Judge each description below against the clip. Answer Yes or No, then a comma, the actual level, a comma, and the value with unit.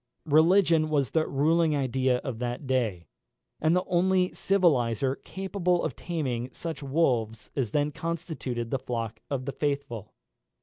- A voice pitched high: No, medium, 140 Hz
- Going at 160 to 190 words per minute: No, average, 140 wpm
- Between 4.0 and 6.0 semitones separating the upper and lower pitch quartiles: Yes, average, 5.2 semitones